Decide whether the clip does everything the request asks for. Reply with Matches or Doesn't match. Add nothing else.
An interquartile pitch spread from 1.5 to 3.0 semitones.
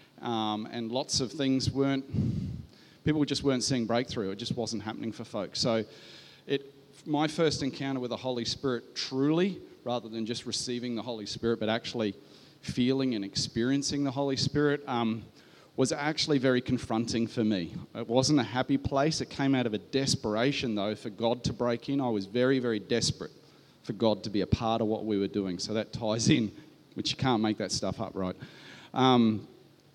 Doesn't match